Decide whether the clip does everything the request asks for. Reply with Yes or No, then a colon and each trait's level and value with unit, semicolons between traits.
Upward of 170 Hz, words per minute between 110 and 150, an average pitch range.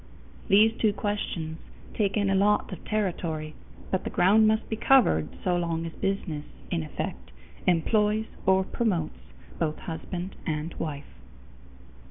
Yes: medium, 185 Hz; average, 140 wpm; average, 4.5 semitones